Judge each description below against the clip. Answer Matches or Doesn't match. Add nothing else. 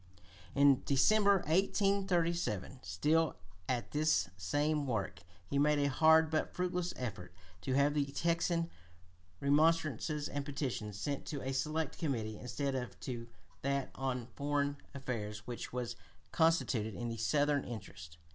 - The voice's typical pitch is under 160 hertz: Matches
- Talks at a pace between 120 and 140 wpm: Matches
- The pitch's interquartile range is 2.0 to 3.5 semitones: Doesn't match